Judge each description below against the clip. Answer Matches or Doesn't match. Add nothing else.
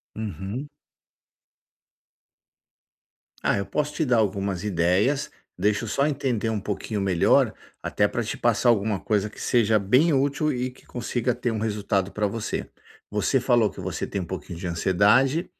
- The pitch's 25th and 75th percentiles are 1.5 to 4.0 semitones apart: Doesn't match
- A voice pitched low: Matches